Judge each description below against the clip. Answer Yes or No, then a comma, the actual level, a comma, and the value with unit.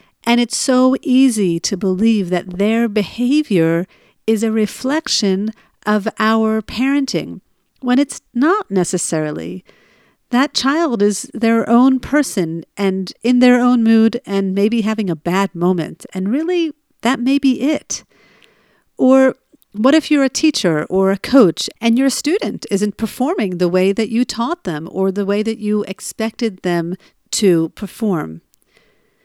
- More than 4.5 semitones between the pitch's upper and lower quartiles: Yes, average, 5.0 semitones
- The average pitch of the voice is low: No, high, 220 Hz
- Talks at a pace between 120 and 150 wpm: Yes, average, 145 wpm